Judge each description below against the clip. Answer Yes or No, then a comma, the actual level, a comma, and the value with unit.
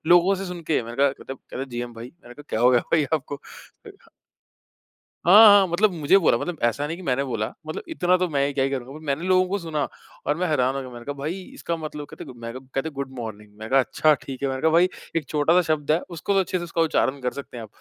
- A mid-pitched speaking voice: Yes, medium, 145 Hz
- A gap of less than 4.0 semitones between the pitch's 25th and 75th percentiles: No, average, 4.6 semitones